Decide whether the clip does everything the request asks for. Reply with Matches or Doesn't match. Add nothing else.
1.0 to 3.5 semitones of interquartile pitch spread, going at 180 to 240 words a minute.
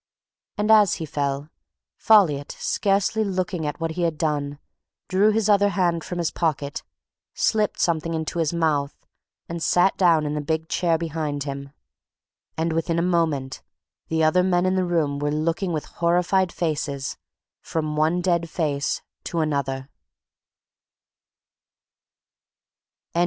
Doesn't match